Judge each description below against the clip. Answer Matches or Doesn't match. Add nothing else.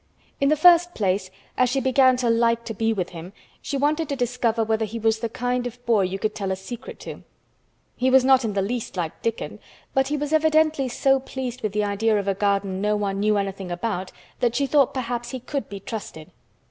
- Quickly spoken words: Matches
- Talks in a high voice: Matches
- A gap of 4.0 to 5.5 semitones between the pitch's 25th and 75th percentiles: Matches